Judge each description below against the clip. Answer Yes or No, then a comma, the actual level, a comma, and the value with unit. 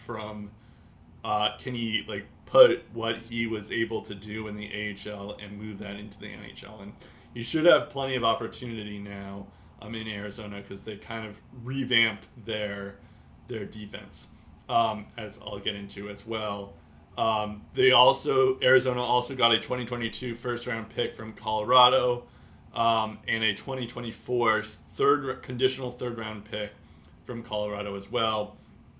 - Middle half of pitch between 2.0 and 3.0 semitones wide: Yes, average, 2.7 semitones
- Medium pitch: No, low, 110 Hz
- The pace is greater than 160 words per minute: No, average, 150 wpm